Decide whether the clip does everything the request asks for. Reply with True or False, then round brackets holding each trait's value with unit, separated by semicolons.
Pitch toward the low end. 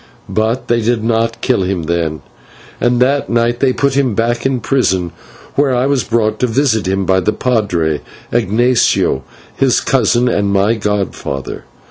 True (115 Hz)